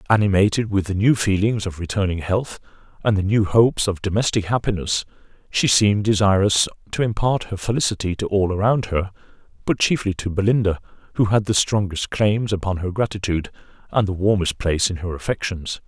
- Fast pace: No, average, 170 wpm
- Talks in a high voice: No, low, 100 Hz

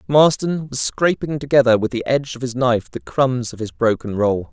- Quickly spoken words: Yes, fast, 210 wpm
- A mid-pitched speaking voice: No, low, 125 Hz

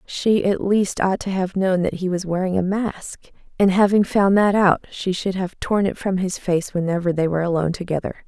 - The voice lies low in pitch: No, medium, 185 Hz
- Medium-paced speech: No, fast, 225 wpm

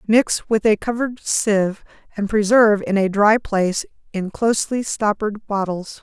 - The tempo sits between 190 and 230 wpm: No, average, 150 wpm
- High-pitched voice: Yes, high, 210 Hz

